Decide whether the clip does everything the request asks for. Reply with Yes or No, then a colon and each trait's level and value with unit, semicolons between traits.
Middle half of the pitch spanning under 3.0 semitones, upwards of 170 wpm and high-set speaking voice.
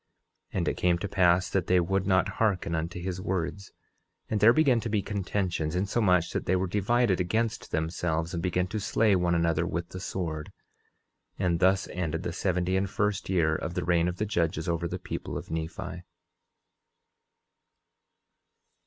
No: narrow, 2.4 semitones; average, 180 wpm; very low, 90 Hz